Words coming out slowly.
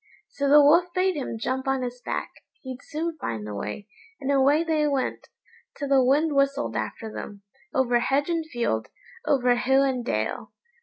No: average, 175 wpm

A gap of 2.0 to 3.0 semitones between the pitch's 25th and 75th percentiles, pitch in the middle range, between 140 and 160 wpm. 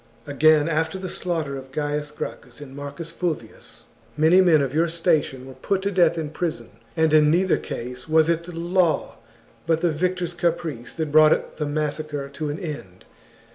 No: narrow, 2.5 semitones; medium, 155 Hz; average, 175 wpm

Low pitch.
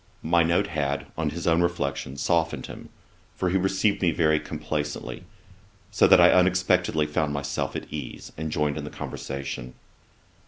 Yes: very low, 80 Hz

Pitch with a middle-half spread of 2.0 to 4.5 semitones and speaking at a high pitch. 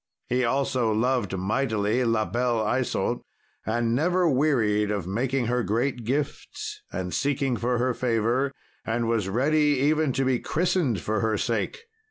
No: average, 3.6 semitones; low, 120 Hz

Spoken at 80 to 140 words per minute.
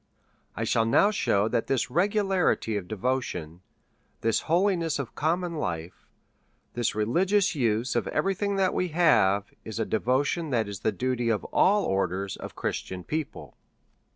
No: average, 155 wpm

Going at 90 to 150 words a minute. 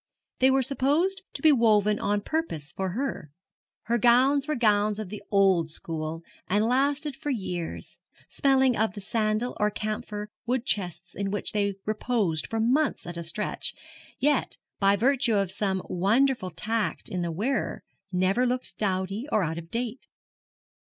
No: average, 160 wpm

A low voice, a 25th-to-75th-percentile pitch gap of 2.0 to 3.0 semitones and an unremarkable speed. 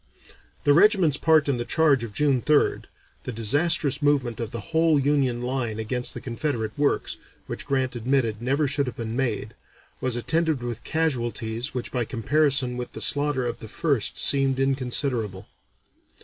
No: low, 130 Hz; average, 3.5 semitones; average, 165 wpm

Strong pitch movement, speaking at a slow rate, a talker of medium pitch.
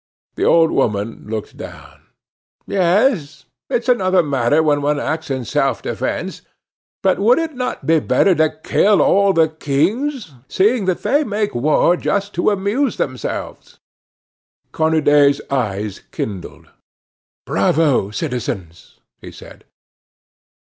Yes: wide, 6.6 semitones; slow, 120 wpm; medium, 160 Hz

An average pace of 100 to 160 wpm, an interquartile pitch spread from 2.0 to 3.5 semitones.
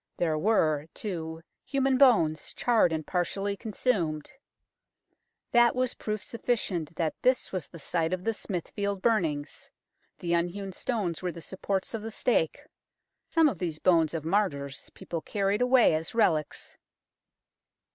No: average, 140 wpm; wide, 5.6 semitones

